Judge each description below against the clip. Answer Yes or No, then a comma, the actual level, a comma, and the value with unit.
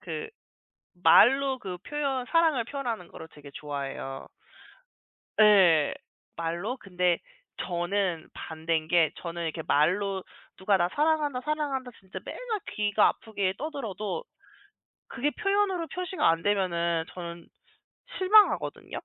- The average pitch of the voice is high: Yes, high, 200 Hz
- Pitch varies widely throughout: Yes, wide, 8.5 semitones